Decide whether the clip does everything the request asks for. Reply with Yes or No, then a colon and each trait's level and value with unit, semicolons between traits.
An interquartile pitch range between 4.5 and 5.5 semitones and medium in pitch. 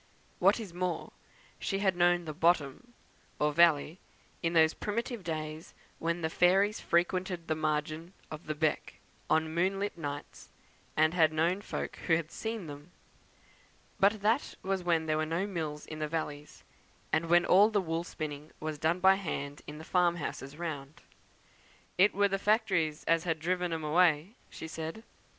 No: average, 2.9 semitones; medium, 165 Hz